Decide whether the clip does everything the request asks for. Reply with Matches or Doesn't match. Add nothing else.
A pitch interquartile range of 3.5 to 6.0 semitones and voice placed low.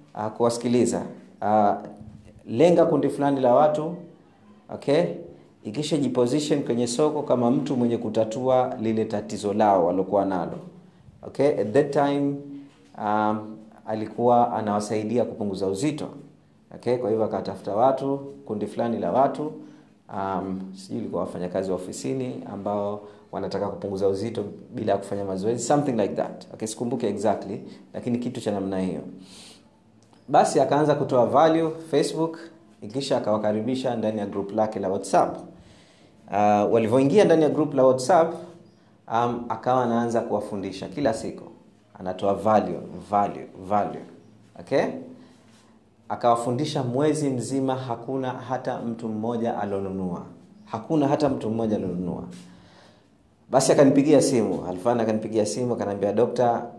Matches